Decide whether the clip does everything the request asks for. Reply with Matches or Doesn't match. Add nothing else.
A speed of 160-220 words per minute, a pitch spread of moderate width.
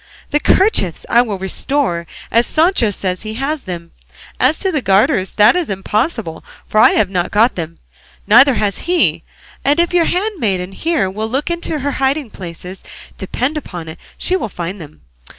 Doesn't match